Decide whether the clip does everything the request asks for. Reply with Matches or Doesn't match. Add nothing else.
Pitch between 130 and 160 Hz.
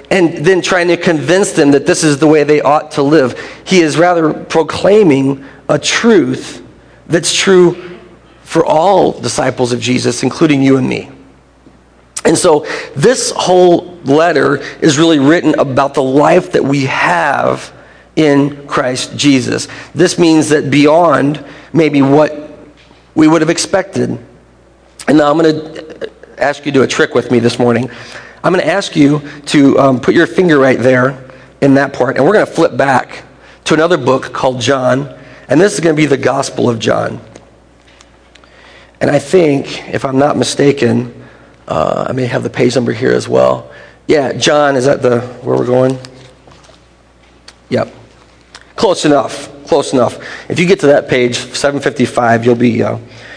Matches